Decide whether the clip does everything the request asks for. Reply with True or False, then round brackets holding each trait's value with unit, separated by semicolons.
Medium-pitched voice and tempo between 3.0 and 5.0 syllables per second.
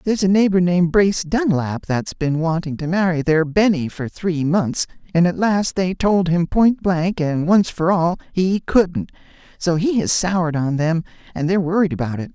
True (175 Hz; 4.8 syllables/s)